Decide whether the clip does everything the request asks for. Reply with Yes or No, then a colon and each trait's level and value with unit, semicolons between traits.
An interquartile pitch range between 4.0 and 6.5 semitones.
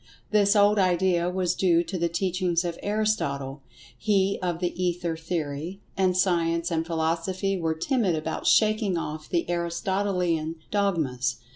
No: average, 2.7 semitones